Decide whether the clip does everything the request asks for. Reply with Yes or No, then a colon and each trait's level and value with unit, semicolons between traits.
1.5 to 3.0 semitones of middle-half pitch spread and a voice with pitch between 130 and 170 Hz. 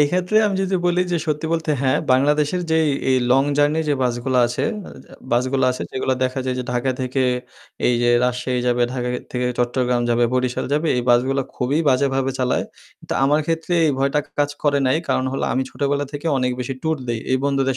Yes: average, 2.7 semitones; low, 135 Hz